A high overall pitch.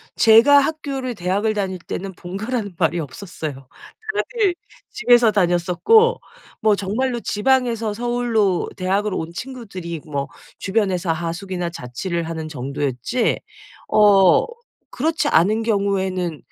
Yes: high, 200 Hz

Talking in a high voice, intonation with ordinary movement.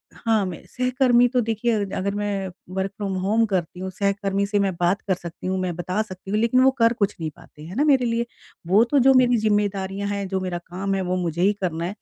Yes: high, 200 Hz; average, 3.5 semitones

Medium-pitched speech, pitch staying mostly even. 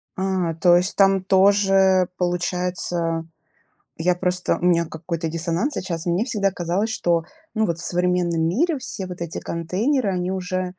Yes: medium, 180 Hz; narrow, 2.1 semitones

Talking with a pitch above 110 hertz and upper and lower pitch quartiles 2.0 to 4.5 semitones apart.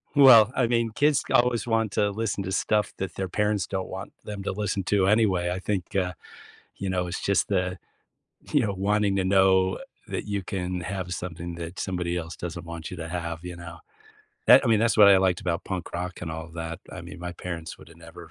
No: very low, 95 Hz; average, 2.8 semitones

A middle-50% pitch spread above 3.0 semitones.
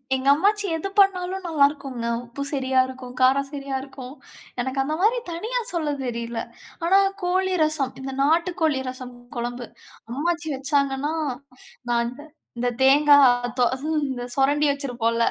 Yes: average, 3.9 semitones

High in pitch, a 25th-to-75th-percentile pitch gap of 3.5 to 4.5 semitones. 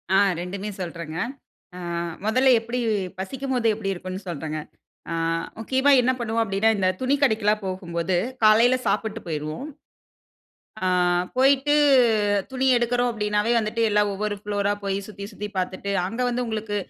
Yes: high, 210 Hz; average, 3.9 semitones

